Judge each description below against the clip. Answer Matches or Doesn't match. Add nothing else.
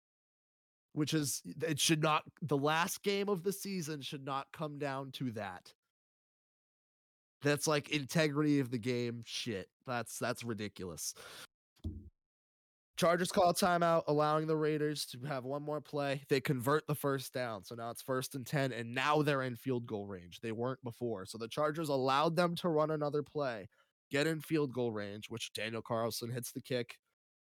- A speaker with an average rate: Matches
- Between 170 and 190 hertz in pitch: Doesn't match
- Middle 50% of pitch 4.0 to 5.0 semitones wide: Matches